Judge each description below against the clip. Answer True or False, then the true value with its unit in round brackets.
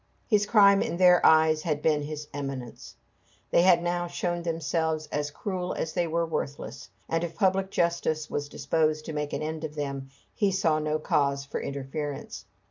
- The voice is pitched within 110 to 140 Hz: False (160 Hz)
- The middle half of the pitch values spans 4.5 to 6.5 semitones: False (2.7 semitones)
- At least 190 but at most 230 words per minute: False (180 wpm)